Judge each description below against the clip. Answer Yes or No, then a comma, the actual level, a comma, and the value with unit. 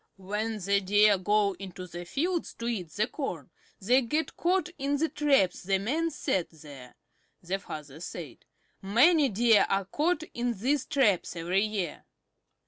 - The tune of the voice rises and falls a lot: Yes, wide, 6.8 semitones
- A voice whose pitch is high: Yes, high, 210 Hz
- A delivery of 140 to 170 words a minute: Yes, average, 155 wpm